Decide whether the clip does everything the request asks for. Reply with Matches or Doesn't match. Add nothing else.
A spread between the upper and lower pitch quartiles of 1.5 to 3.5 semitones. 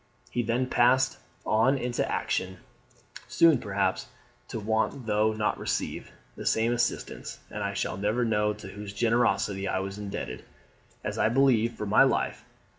Matches